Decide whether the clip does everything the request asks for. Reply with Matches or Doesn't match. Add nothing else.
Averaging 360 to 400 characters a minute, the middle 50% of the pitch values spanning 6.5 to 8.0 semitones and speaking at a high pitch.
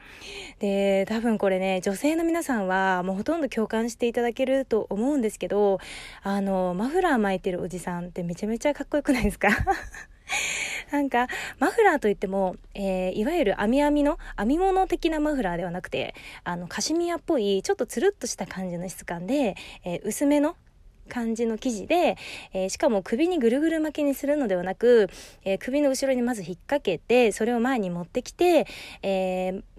Matches